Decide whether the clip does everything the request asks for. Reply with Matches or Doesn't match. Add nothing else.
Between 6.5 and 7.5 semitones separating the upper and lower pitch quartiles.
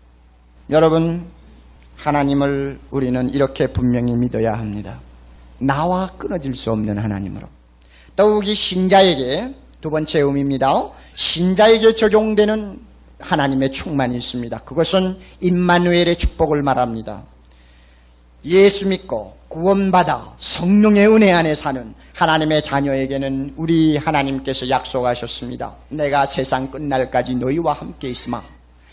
Matches